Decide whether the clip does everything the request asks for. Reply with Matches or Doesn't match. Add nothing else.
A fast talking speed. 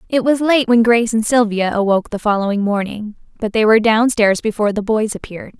Matches